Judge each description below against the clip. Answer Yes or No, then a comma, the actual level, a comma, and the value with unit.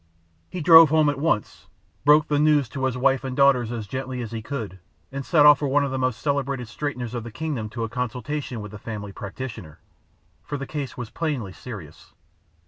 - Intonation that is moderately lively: Yes, average, 4.1 semitones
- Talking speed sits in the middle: No, fast, 210 wpm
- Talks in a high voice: No, low, 130 Hz